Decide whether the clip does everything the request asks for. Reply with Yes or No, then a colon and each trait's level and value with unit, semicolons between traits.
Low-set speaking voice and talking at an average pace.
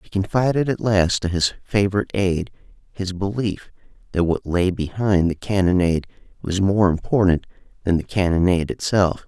Yes: very low, 95 Hz; average, 150 wpm